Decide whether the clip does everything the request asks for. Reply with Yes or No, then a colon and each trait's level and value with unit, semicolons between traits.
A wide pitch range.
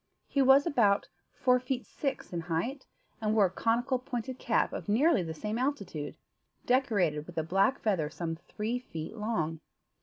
Yes: wide, 6.8 semitones